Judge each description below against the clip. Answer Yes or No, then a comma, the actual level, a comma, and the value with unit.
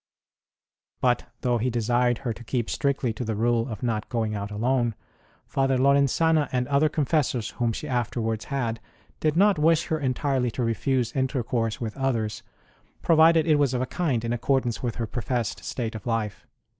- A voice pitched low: Yes, low, 125 Hz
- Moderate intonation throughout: Yes, average, 3.3 semitones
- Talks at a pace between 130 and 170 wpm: No, average, 180 wpm